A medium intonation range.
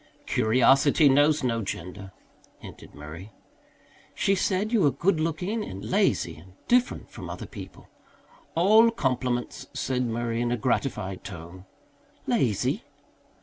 No: wide, 8.3 semitones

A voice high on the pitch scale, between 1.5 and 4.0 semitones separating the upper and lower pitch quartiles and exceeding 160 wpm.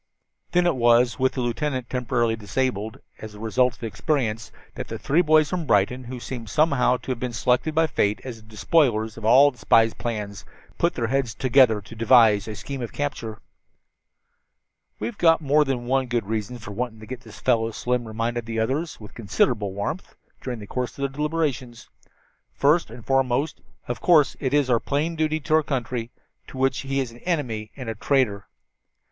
No: low, 125 Hz; average, 3.7 semitones; average, 195 wpm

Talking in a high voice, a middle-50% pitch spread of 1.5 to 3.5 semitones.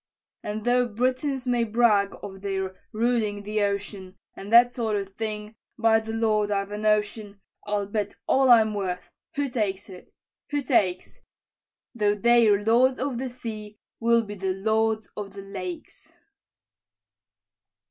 Yes: high, 215 Hz; average, 2.7 semitones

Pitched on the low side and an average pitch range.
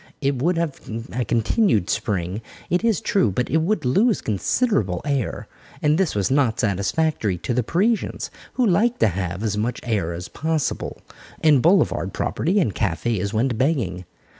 No: low, 125 Hz; wide, 8.6 semitones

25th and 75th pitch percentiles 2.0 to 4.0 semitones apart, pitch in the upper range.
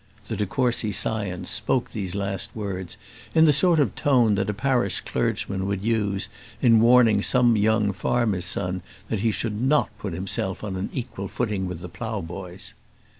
No: average, 3.6 semitones; low, 105 Hz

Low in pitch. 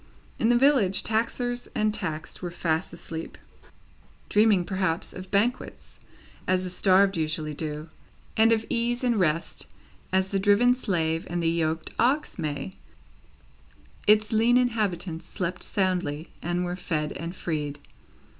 No: medium, 185 Hz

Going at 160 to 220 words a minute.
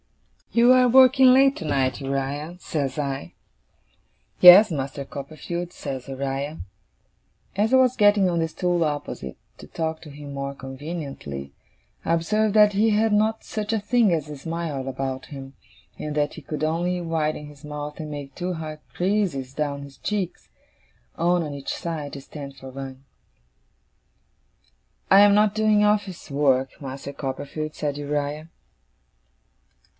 No: average, 150 wpm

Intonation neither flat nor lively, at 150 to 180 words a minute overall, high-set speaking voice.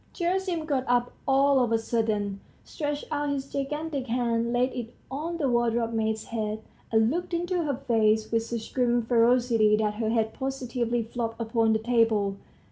Yes: average, 3.5 semitones; average, 170 wpm; high, 240 Hz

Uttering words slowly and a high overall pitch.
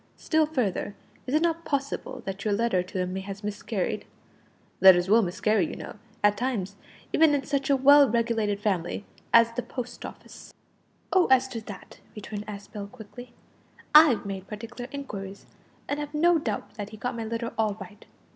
No: average, 175 wpm; high, 225 Hz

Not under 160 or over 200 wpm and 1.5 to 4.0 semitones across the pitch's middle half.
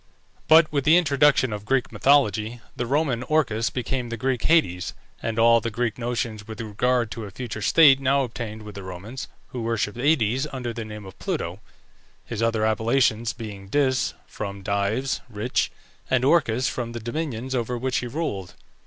Yes: average, 175 wpm; average, 3.5 semitones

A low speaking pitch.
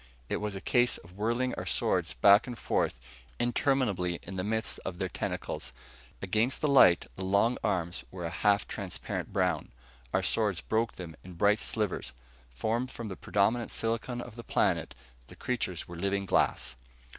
Yes: low, 100 Hz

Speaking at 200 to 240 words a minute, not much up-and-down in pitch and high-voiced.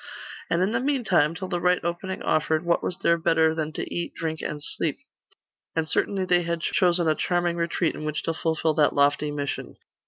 No: fast, 205 wpm; narrow, 2.0 semitones; medium, 170 Hz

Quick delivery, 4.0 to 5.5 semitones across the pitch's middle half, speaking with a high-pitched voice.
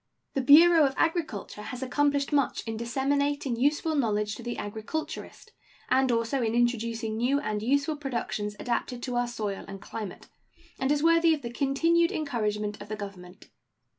No: average, 165 wpm; average, 4.7 semitones; high, 245 Hz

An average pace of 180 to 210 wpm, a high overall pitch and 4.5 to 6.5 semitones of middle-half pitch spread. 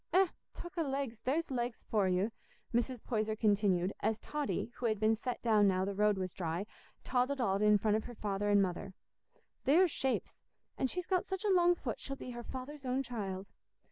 Yes: fast, 205 wpm; high, 230 Hz; average, 4.8 semitones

